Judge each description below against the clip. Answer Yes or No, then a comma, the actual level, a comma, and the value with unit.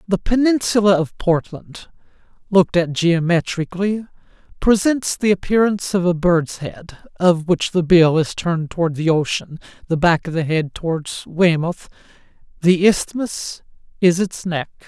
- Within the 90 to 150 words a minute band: Yes, average, 140 wpm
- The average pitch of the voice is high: No, medium, 175 Hz